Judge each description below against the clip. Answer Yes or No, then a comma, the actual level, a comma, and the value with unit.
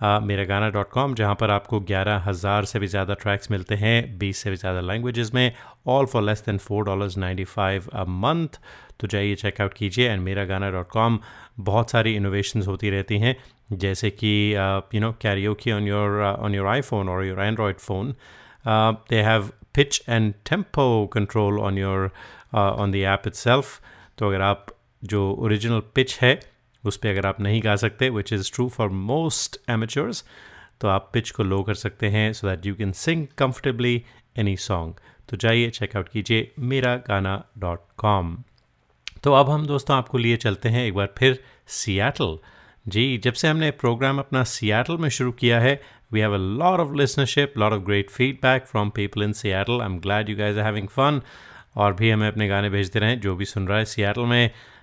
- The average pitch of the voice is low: Yes, low, 105 Hz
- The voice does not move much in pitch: No, average, 3.4 semitones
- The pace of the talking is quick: Yes, fast, 195 wpm